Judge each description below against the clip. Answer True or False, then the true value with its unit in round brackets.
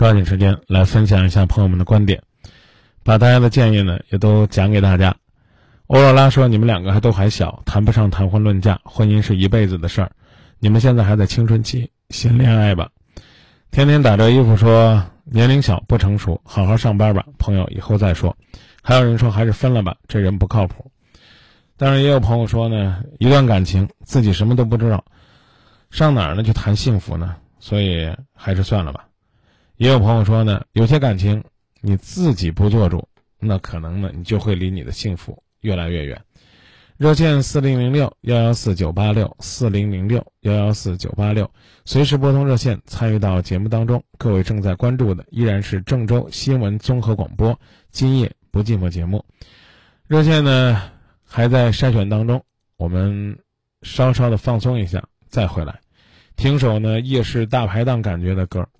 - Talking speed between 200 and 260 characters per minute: False (275 characters per minute)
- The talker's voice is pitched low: True (110 Hz)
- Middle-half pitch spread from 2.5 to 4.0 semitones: True (3.7 semitones)